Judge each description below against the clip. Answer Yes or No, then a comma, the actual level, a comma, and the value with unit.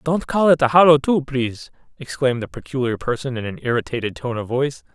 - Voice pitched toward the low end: Yes, low, 130 Hz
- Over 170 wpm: Yes, fast, 205 wpm